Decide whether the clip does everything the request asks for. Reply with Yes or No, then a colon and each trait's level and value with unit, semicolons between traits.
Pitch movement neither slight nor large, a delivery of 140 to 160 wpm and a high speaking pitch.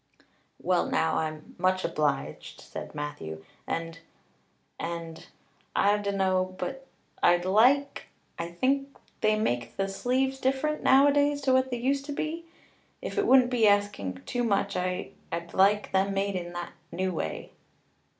No: wide, 7.4 semitones; average, 145 wpm; high, 200 Hz